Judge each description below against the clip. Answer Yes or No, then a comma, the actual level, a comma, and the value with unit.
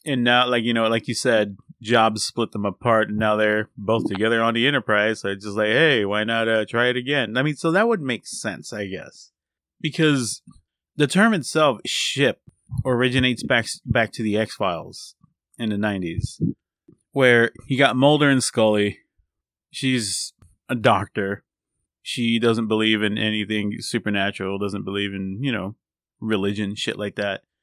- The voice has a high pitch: No, low, 110 Hz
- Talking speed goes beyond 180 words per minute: No, average, 170 wpm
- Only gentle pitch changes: No, average, 3.4 semitones